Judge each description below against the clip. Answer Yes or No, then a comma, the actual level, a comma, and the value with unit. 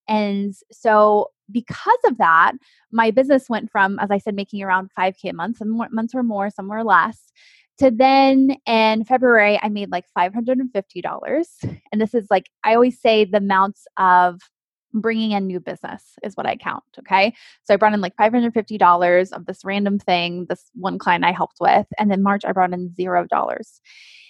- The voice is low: No, high, 210 Hz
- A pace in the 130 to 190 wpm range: No, fast, 205 wpm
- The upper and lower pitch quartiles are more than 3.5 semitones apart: No, average, 3.2 semitones